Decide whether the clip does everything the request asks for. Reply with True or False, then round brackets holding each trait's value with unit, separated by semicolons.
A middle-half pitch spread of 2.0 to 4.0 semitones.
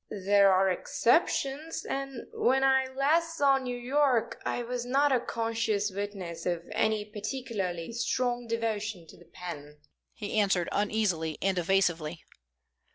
False (5.3 semitones)